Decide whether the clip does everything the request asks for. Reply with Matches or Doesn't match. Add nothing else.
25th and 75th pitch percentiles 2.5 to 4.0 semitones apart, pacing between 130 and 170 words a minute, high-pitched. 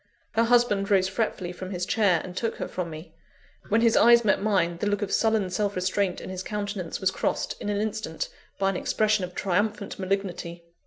Doesn't match